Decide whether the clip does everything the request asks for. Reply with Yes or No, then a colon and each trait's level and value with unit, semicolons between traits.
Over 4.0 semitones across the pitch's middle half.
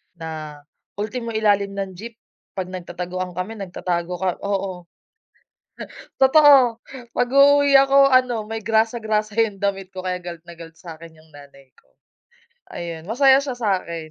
Yes: average, 5.1 semitones